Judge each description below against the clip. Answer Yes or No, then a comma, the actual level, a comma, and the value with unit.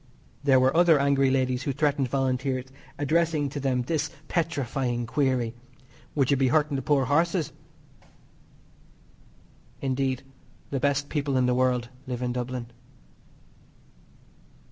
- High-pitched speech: No, low, 135 Hz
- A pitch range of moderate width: No, narrow, 2.2 semitones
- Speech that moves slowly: Yes, slow, 125 wpm